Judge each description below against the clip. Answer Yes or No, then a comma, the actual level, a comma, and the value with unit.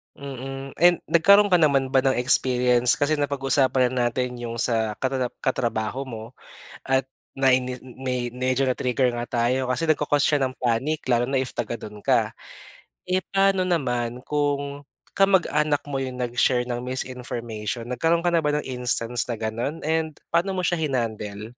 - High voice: No, low, 130 Hz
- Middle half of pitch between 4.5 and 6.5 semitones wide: No, average, 3.2 semitones